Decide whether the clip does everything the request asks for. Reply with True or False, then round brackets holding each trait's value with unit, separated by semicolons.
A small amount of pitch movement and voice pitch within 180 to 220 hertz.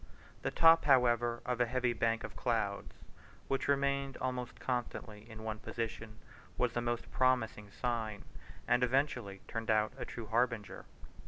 False (2.3 semitones; 120 Hz)